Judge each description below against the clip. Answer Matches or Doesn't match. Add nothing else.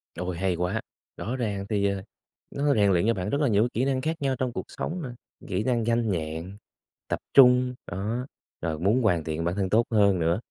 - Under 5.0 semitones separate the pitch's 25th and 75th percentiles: Doesn't match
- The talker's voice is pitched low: Matches